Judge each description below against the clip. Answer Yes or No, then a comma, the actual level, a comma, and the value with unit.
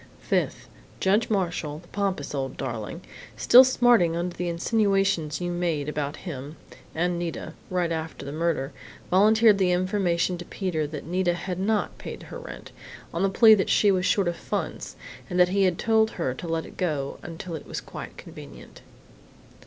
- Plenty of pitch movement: No, average, 3.4 semitones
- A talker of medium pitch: Yes, medium, 175 Hz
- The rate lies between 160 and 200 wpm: Yes, average, 175 wpm